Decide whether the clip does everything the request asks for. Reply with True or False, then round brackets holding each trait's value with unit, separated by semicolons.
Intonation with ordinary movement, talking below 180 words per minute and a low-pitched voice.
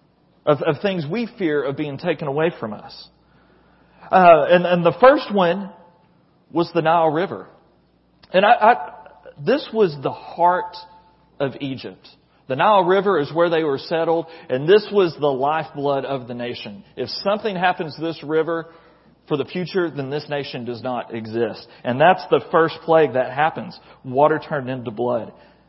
False (3.9 semitones; 170 wpm; 165 Hz)